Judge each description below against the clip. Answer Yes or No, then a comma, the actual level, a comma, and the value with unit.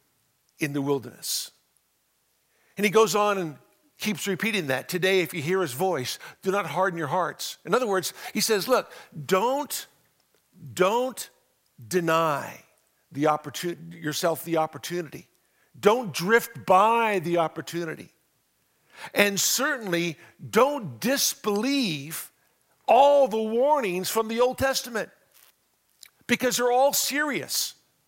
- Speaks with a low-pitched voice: No, medium, 185 Hz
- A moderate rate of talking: No, slow, 115 wpm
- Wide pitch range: Yes, wide, 5.7 semitones